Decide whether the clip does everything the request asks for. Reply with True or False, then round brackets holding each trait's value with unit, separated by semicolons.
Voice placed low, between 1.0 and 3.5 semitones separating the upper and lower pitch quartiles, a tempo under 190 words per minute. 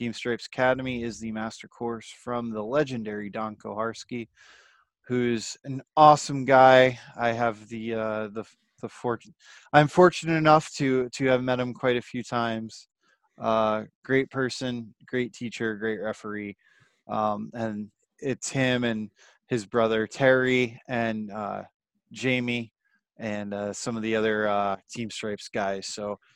True (115 Hz; 2.9 semitones; 145 wpm)